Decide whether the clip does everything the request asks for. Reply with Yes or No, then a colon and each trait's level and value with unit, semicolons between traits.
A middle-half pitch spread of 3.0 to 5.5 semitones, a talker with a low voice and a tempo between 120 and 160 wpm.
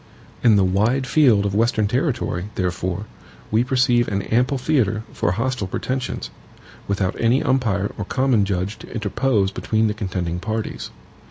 Yes: average, 4.2 semitones; low, 110 Hz; average, 150 wpm